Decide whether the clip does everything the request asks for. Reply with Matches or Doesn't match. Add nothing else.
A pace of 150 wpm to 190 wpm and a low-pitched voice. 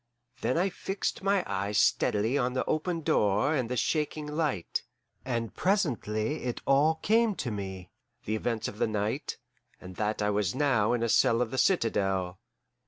Matches